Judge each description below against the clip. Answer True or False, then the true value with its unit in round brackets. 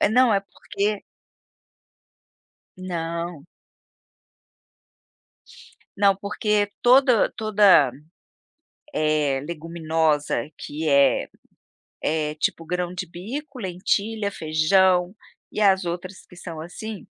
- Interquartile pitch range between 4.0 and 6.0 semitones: True (4.3 semitones)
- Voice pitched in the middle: True (180 Hz)